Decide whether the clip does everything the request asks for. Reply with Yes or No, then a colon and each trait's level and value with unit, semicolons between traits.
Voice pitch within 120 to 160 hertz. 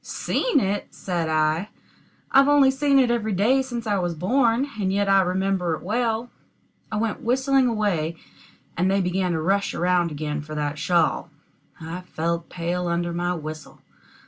No: high, 190 Hz